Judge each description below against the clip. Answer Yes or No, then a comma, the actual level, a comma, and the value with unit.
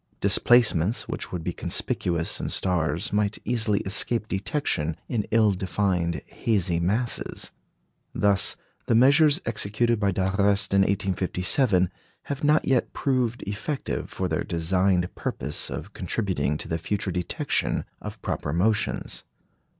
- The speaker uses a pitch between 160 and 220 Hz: No, low, 100 Hz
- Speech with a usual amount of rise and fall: Yes, average, 4.2 semitones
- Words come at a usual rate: No, slow, 125 wpm